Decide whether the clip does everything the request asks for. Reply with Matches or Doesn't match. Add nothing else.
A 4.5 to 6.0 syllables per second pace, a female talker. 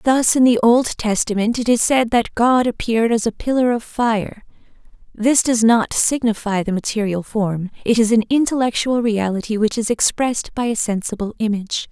Matches